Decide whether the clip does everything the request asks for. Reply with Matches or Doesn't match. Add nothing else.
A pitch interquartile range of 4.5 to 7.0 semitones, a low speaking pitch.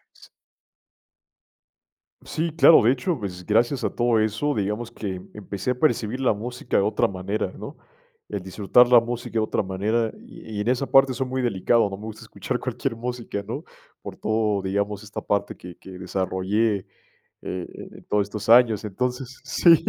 Doesn't match